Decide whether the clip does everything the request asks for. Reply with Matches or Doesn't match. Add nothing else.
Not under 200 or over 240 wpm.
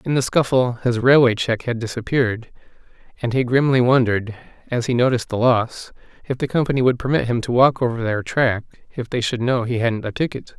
Matches